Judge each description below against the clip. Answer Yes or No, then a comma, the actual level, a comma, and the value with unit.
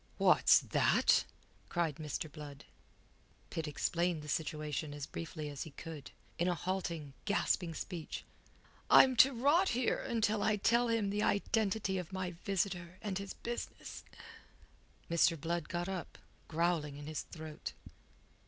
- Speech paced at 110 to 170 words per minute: Yes, average, 140 wpm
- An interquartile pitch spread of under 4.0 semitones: No, average, 4.4 semitones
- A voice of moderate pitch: Yes, medium, 175 Hz